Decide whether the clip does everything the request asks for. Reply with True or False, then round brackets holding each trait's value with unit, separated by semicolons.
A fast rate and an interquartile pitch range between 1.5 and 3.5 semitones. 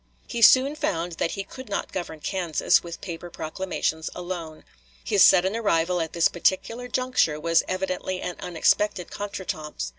False (150 wpm; 3.2 semitones)